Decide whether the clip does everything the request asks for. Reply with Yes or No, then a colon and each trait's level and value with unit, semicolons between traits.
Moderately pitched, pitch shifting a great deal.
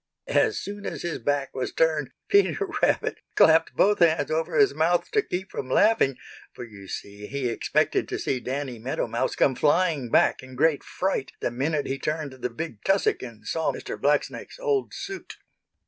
Yes: medium, 150 Hz; wide, 5.7 semitones